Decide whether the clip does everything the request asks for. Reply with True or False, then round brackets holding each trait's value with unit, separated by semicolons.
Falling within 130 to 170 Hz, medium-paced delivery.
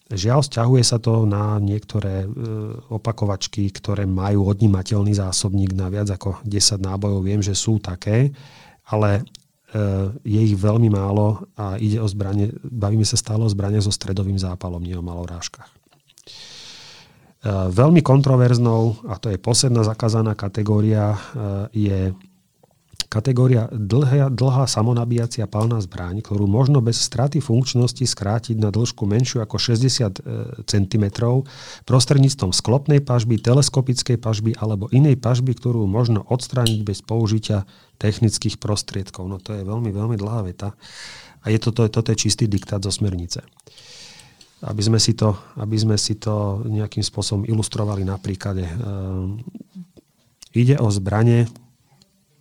False (110 Hz; 130 wpm)